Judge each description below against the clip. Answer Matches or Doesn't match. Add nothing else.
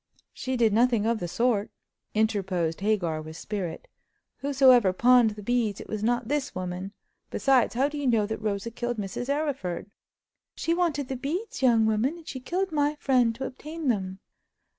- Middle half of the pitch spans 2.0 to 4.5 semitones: Doesn't match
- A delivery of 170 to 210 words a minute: Matches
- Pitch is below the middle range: Doesn't match